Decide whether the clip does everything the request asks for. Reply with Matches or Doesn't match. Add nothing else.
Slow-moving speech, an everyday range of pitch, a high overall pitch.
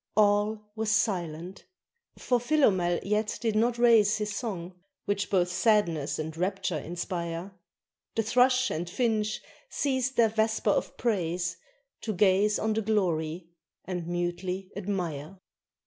Matches